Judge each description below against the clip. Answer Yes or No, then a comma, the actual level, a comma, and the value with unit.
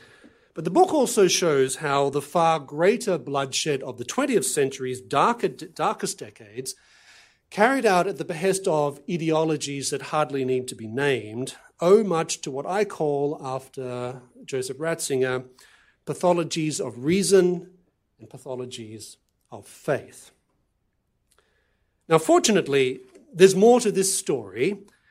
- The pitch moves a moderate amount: No, wide, 6.3 semitones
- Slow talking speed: Yes, slow, 125 wpm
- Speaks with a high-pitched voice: No, medium, 155 Hz